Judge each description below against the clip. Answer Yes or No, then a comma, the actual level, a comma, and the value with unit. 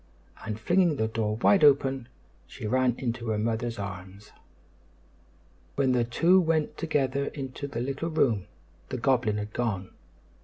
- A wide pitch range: No, average, 4.2 semitones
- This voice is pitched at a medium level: No, low, 120 Hz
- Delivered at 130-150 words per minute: Yes, average, 145 wpm